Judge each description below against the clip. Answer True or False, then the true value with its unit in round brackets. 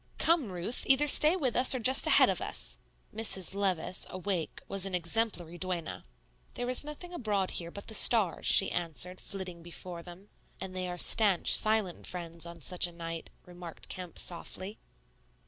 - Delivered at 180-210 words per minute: False (170 wpm)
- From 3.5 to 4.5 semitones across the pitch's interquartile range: True (4.2 semitones)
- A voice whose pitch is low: False (185 Hz)